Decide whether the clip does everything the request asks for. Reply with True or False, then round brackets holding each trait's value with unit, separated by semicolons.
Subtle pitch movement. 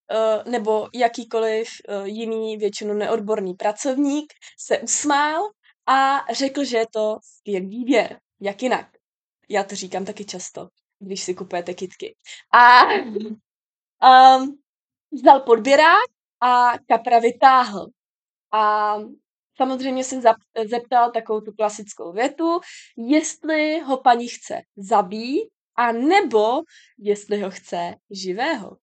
False (4.2 semitones)